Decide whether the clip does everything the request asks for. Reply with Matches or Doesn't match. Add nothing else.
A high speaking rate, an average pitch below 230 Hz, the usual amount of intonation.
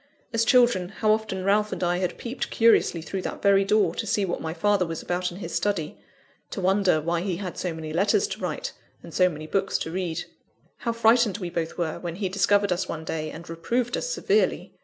Matches